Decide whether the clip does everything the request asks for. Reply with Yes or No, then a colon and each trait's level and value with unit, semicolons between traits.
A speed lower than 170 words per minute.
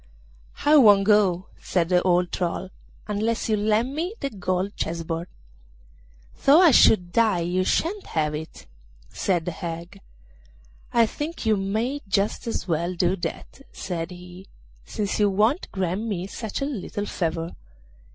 Yes: average, 150 wpm